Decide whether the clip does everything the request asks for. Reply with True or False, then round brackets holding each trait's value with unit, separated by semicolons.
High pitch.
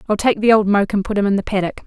True (205 Hz)